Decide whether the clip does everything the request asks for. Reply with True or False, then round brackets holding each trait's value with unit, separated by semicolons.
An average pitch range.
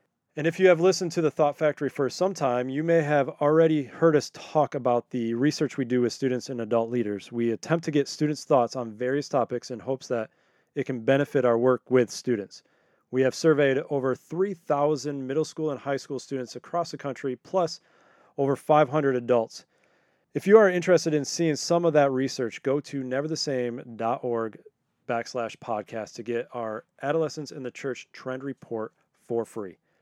True (3.7 semitones)